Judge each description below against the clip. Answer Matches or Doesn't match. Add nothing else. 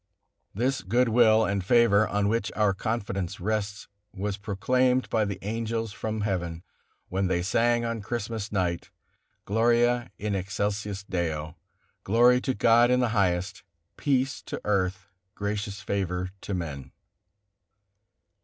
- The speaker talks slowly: Matches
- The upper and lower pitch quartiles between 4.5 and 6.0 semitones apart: Doesn't match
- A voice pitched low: Matches